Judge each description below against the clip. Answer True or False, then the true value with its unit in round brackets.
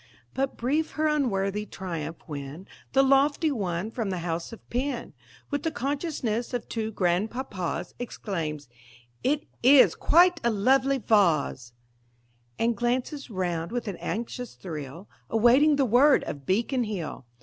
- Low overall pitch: False (230 Hz)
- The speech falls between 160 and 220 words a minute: False (140 wpm)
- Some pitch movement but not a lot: False (6.9 semitones)